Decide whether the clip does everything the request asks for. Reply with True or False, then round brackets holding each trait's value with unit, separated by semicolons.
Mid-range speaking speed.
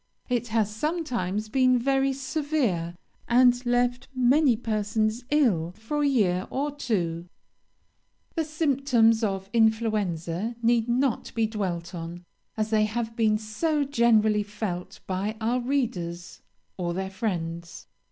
False (125 wpm)